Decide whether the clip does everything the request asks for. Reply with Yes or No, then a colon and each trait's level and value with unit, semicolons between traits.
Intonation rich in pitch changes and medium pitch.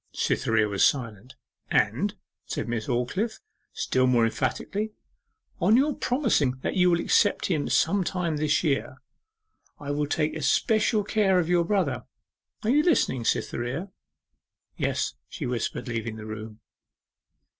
Yes: wide, 8.9 semitones; medium, 150 Hz